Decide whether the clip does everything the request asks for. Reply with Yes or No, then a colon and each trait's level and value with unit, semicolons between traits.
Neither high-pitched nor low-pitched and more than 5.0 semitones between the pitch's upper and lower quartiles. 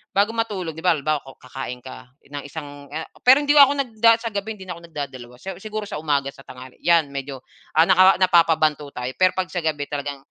Yes: medium, 160 Hz; wide, 5.4 semitones